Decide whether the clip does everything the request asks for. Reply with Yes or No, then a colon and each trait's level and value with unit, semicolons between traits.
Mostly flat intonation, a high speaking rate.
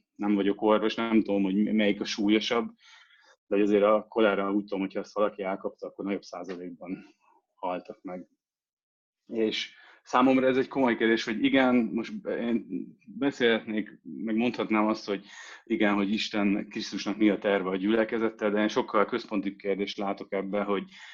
Yes: narrow, 2.0 semitones; fast, 160 wpm